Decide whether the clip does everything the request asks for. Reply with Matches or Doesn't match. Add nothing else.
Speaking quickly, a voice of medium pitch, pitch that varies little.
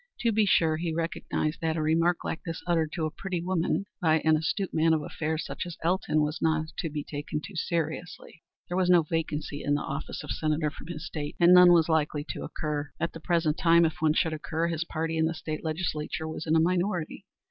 Matches